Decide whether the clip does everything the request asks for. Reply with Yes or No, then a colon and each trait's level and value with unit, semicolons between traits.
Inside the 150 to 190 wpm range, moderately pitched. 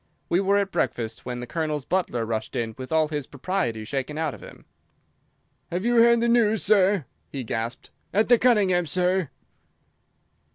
Yes: average, 170 wpm; medium, 165 Hz